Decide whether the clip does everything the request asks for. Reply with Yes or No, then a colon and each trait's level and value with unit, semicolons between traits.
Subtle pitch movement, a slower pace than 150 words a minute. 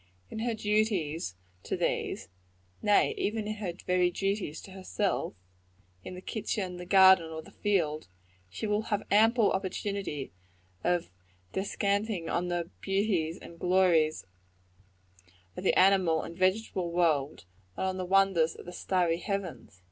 No: average, 3.0 semitones; average, 140 wpm